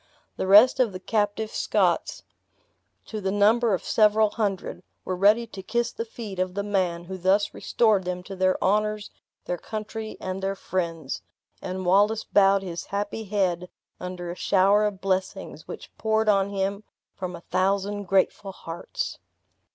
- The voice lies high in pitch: Yes, high, 195 Hz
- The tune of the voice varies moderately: No, narrow, 2.2 semitones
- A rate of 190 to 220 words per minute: No, average, 160 wpm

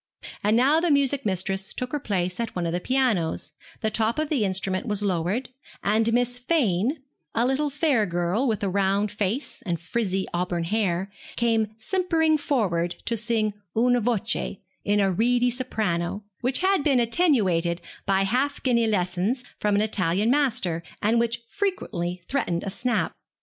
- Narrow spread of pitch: No, average, 4.9 semitones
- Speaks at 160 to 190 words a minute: Yes, average, 165 wpm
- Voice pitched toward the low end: No, high, 220 Hz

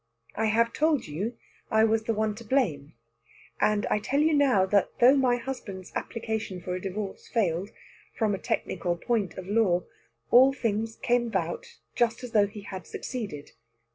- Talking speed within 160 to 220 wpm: Yes, average, 170 wpm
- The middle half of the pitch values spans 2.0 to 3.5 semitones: No, average, 3.9 semitones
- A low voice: No, high, 220 Hz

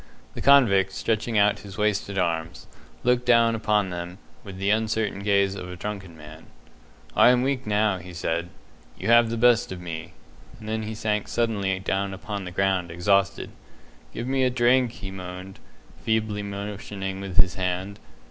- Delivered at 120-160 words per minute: No, average, 170 wpm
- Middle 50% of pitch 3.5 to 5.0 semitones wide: No, average, 2.9 semitones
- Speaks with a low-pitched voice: Yes, low, 100 Hz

